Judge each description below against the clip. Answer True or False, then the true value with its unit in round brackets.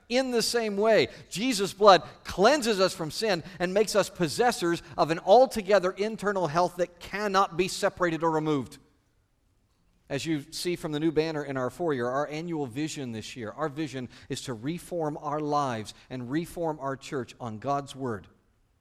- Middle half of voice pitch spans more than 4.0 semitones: True (5.6 semitones)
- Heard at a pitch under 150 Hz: False (160 Hz)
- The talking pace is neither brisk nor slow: True (170 wpm)